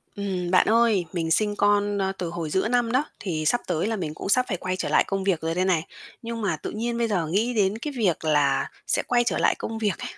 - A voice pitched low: No, high, 195 Hz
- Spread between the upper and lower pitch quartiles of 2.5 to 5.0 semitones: Yes, average, 4.6 semitones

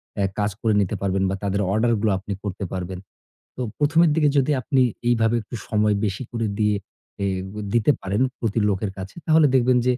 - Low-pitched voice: Yes, low, 110 Hz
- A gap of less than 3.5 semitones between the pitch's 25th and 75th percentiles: No, average, 4.0 semitones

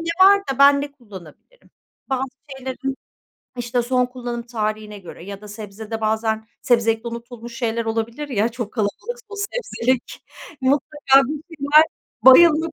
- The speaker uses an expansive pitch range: No, average, 4.1 semitones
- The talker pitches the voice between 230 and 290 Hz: Yes, high, 245 Hz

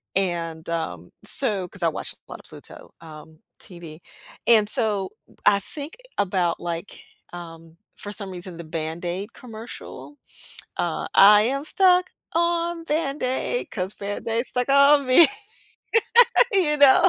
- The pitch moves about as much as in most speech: No, wide, 8.3 semitones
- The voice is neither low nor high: No, high, 205 Hz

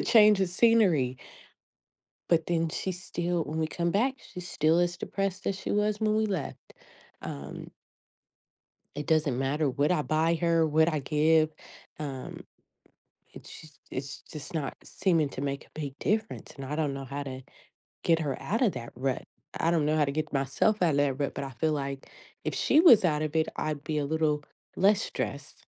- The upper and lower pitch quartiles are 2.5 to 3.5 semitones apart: No, average, 3.9 semitones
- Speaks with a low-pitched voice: No, medium, 155 Hz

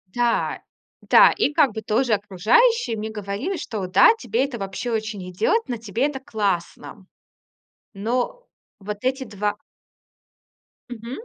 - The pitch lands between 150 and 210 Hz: No, high, 225 Hz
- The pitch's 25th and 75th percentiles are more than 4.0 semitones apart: Yes, average, 4.4 semitones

